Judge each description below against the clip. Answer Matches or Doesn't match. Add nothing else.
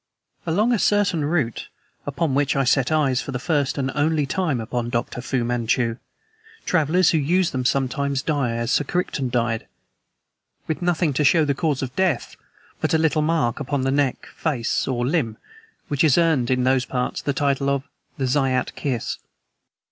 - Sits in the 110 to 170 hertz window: Matches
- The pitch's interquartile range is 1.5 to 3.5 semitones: Doesn't match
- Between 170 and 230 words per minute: Matches